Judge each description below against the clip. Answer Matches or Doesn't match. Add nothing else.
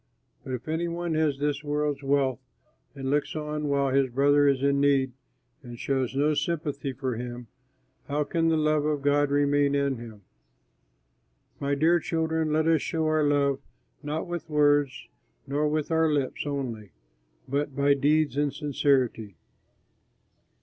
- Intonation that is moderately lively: Doesn't match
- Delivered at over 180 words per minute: Doesn't match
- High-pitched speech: Doesn't match